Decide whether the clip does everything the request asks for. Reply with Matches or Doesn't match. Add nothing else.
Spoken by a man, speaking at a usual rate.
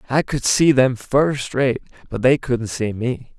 Matches